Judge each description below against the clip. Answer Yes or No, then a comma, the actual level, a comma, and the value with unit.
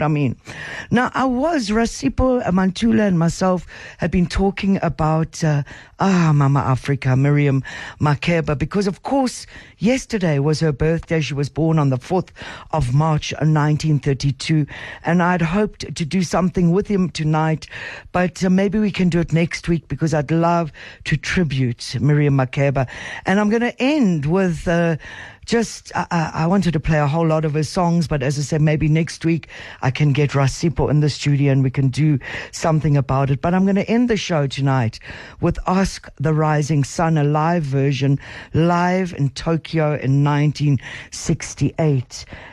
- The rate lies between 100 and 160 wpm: No, average, 170 wpm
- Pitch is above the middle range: No, medium, 155 Hz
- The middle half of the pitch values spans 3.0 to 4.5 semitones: Yes, average, 3.9 semitones